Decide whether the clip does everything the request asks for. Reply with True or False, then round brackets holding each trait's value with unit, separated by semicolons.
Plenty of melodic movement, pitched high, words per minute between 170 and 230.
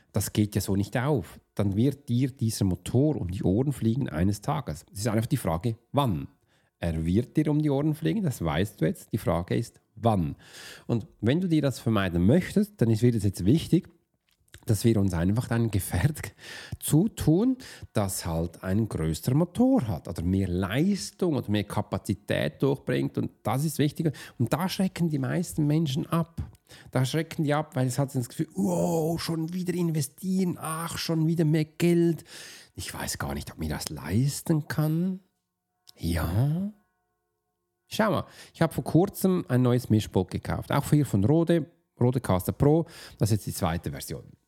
False (7.8 semitones; 130 Hz; 175 wpm)